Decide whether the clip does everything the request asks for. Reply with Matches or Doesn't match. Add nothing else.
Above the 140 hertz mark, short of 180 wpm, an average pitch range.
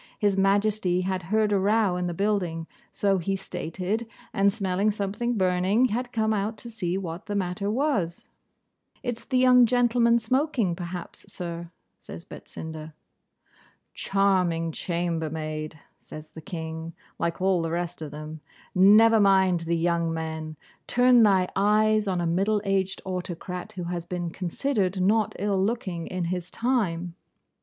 Matches